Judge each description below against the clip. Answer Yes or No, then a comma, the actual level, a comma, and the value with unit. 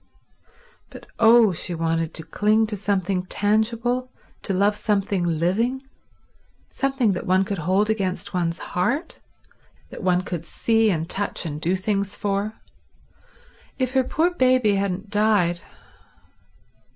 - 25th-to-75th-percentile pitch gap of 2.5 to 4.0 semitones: Yes, average, 3.6 semitones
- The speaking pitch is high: Yes, high, 200 Hz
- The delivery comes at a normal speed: No, slow, 130 wpm